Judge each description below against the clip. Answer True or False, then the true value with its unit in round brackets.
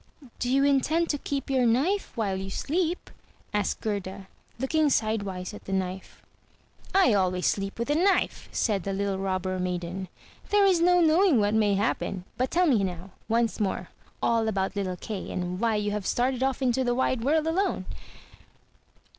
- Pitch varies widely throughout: True (6.3 semitones)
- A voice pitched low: False (220 Hz)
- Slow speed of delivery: False (175 wpm)